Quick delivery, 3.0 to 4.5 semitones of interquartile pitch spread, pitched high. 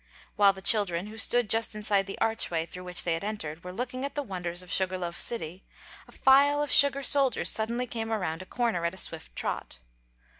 No: fast, 215 wpm; average, 5.1 semitones; high, 205 Hz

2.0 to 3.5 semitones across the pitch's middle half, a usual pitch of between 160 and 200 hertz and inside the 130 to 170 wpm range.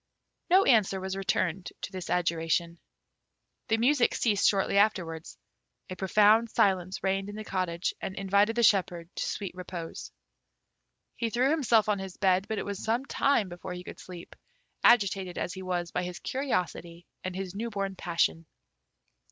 Yes: average, 3.1 semitones; high, 190 Hz; average, 165 wpm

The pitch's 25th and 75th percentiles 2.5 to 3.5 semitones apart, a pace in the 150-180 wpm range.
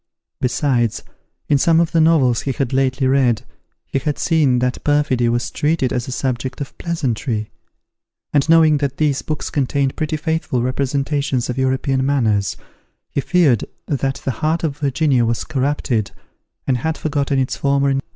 Yes: average, 2.8 semitones; average, 160 wpm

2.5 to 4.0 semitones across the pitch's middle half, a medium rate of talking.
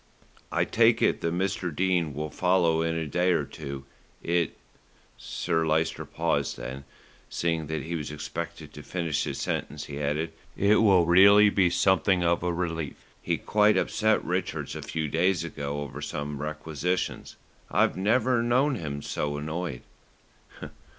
Yes: average, 3.7 semitones; average, 155 wpm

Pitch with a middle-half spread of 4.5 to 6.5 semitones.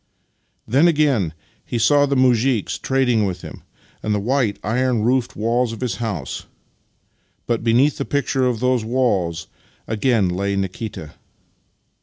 No: average, 3.9 semitones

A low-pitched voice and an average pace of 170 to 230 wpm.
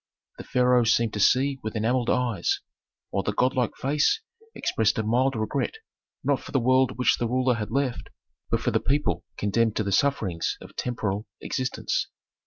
Yes: low, 120 Hz; average, 175 wpm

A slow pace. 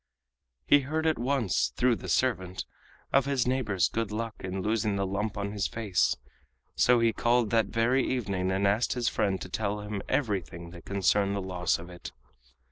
No: average, 185 wpm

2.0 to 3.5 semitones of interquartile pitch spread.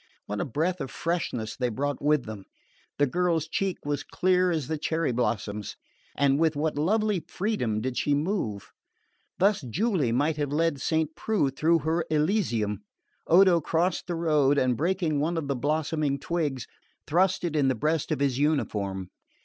No: average, 4.2 semitones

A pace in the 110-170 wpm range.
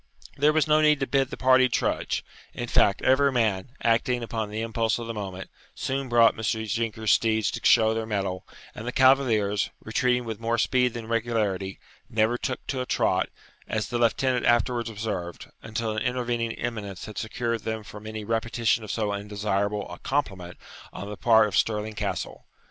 No: average, 180 wpm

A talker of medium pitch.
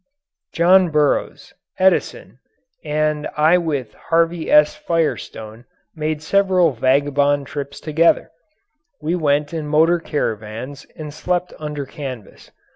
Yes: medium, 150 Hz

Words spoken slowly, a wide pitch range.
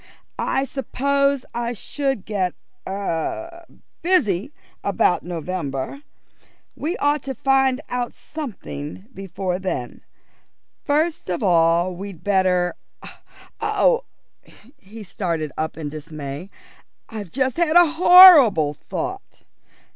Yes: slow, 100 wpm; wide, 8.0 semitones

